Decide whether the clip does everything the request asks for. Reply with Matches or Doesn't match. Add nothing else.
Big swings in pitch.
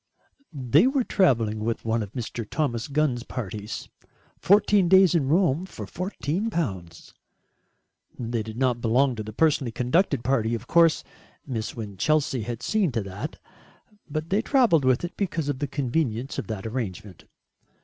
Matches